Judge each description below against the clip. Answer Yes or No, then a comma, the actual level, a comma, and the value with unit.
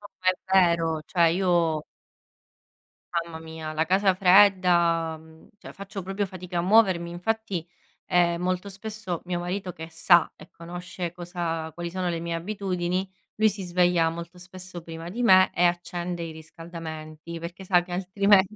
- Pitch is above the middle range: No, medium, 175 Hz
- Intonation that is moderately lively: No, narrow, 2.0 semitones